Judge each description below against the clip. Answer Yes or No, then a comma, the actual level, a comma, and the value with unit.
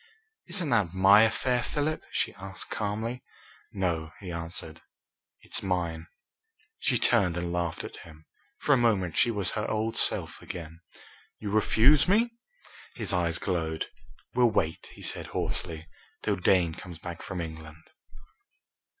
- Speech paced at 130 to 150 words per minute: Yes, average, 140 wpm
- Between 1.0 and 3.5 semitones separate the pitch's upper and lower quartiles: No, average, 5.2 semitones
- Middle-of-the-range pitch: No, very low, 95 Hz